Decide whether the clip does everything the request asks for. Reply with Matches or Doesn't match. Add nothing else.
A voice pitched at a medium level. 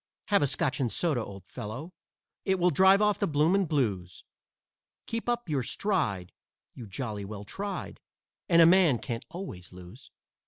Matches